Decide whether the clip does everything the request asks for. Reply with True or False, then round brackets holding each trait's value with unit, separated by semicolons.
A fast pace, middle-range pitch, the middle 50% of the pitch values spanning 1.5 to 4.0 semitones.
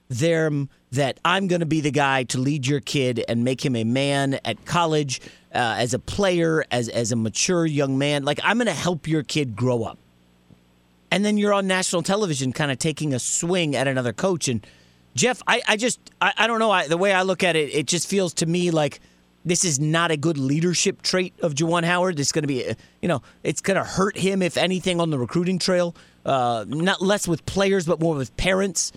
False (230 wpm; 160 Hz; 5.2 semitones)